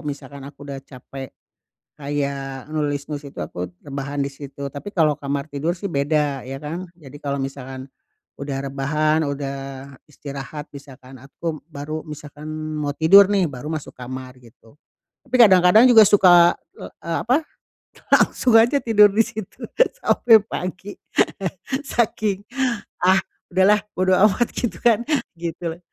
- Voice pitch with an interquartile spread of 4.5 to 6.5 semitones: Yes, average, 5.0 semitones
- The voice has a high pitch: No, medium, 150 Hz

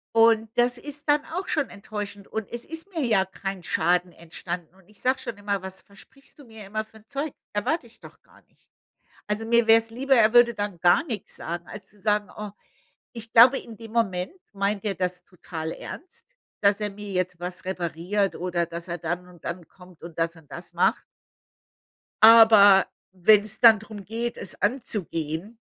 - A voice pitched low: No, high, 205 Hz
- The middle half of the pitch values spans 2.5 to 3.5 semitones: No, average, 4.0 semitones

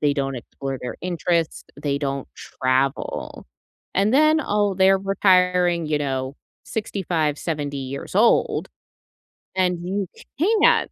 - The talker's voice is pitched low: No, medium, 170 Hz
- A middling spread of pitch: No, wide, 5.8 semitones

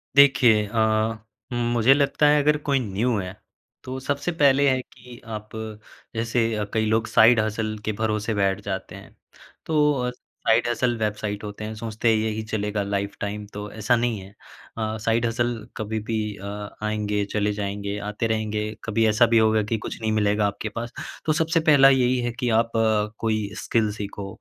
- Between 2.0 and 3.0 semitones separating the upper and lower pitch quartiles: Yes, narrow, 2.4 semitones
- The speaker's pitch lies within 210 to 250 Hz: No, low, 110 Hz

